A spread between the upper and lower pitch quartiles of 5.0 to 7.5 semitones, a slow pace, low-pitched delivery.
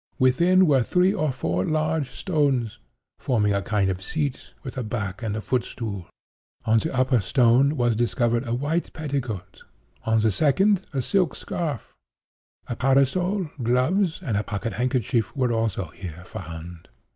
No: wide, 5.4 semitones; average, 150 wpm; low, 125 Hz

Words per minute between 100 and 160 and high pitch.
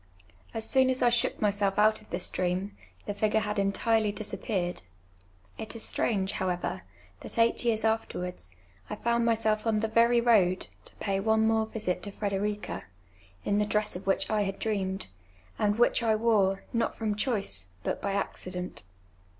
No: average, 175 wpm; high, 210 Hz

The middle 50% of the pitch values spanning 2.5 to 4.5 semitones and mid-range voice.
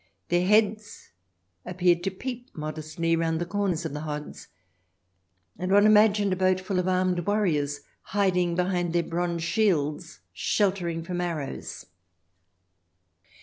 Yes: average, 2.9 semitones; medium, 180 Hz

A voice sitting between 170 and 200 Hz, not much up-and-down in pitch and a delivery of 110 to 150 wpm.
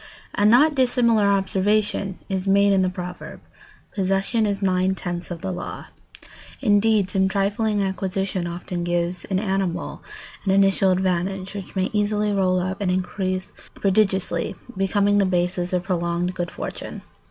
Yes: high, 190 Hz; narrow, 1.8 semitones; average, 145 wpm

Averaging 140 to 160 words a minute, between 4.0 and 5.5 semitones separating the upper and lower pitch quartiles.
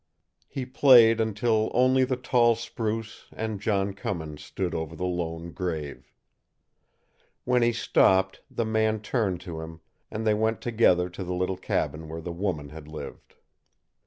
Yes: average, 155 wpm; average, 4.8 semitones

